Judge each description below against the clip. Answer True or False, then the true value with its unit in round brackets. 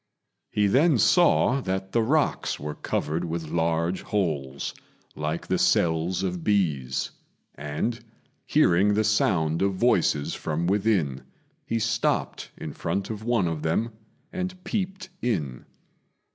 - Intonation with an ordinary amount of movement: False (6.0 semitones)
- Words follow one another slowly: True (130 wpm)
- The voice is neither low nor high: False (95 Hz)